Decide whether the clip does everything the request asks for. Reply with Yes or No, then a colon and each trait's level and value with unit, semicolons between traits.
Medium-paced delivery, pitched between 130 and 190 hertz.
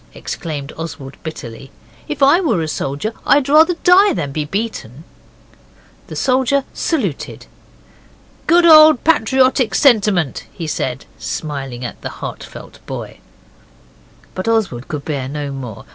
No: slow, 130 wpm; medium, 185 Hz